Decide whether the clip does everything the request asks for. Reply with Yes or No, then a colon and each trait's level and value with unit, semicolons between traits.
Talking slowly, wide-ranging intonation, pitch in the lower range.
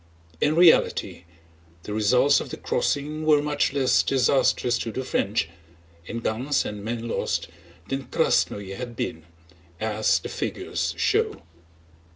Yes: slow, 125 wpm; wide, 5.8 semitones; low, 115 Hz